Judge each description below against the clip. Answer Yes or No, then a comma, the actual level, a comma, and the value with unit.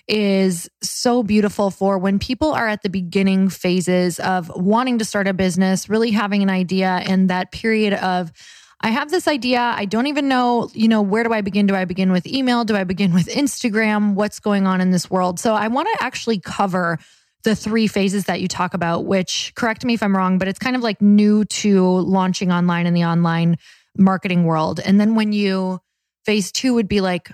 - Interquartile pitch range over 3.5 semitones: No, average, 3.0 semitones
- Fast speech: Yes, fast, 215 wpm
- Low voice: No, high, 195 Hz